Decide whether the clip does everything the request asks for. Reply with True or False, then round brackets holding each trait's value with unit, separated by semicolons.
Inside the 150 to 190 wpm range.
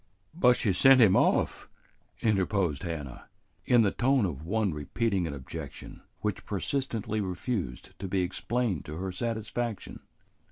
False (135 wpm)